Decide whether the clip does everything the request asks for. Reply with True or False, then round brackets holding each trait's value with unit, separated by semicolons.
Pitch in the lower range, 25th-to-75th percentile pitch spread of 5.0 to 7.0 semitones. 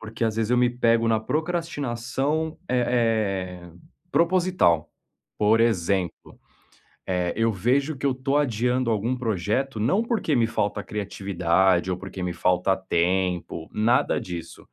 True (115 Hz; 5.5 semitones)